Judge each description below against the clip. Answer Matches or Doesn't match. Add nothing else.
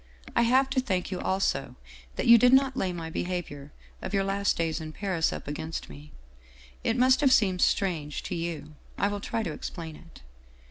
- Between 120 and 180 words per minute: Doesn't match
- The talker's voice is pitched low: Doesn't match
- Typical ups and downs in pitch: Doesn't match